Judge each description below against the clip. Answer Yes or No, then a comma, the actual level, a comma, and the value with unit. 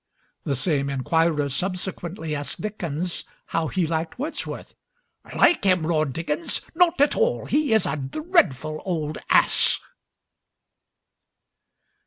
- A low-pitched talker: No, medium, 165 Hz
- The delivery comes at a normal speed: No, slow, 115 wpm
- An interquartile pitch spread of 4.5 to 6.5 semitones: Yes, average, 5.2 semitones